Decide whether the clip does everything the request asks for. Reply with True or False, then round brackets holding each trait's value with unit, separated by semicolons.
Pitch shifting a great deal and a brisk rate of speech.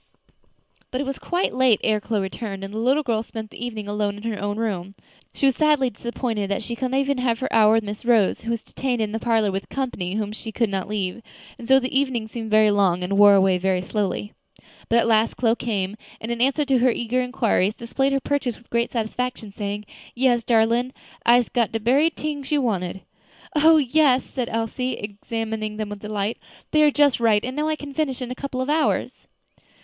False (3.7 semitones; 225 wpm)